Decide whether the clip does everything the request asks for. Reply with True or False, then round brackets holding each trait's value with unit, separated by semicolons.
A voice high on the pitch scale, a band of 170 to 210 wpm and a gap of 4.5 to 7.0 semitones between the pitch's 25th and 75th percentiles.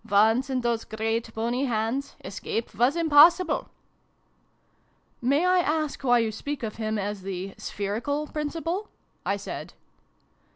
False (245 Hz; 150 wpm; 5.2 semitones)